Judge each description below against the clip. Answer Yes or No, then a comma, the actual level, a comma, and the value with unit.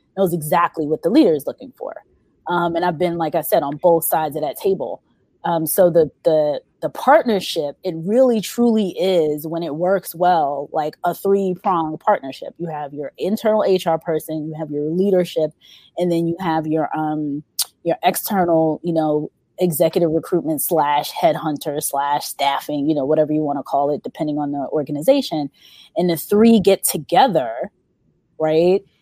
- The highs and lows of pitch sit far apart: No, average, 3.3 semitones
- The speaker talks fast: No, average, 175 wpm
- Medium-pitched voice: Yes, medium, 165 Hz